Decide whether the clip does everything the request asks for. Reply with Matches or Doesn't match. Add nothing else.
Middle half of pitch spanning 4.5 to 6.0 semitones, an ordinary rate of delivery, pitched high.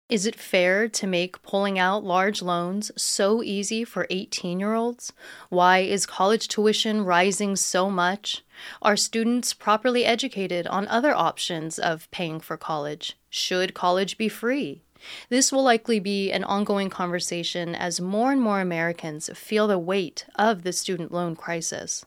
Doesn't match